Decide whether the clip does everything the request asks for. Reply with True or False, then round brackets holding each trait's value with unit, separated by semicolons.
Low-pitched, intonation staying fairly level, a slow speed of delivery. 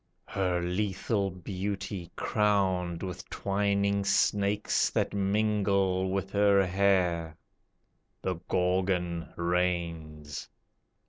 True (95 Hz; 2.1 semitones; 80 wpm)